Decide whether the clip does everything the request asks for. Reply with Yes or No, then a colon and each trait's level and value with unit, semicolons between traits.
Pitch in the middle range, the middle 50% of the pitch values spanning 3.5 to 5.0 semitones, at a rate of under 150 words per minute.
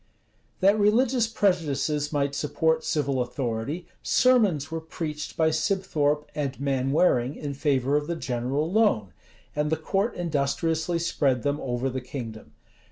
Yes: medium, 150 Hz; average, 3.8 semitones; slow, 135 wpm